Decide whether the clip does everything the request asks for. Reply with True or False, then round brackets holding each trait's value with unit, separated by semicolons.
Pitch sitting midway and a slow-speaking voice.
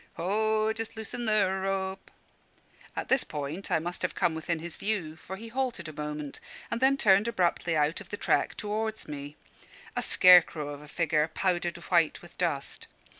False (180 Hz; 180 wpm)